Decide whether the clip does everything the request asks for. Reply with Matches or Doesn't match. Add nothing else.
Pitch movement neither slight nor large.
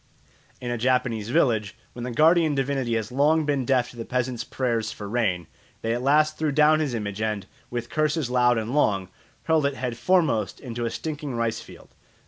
Matches